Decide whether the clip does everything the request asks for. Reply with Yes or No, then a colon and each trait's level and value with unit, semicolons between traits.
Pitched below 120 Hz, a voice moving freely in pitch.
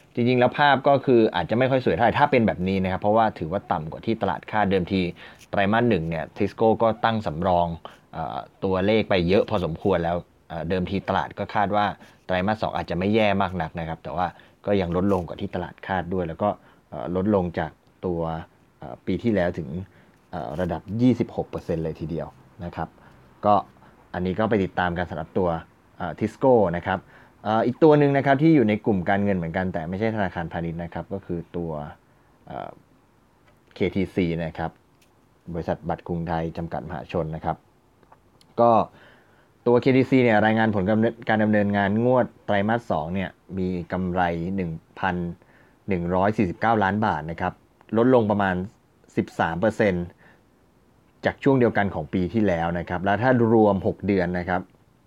No: very low, 95 Hz; average, 4.2 semitones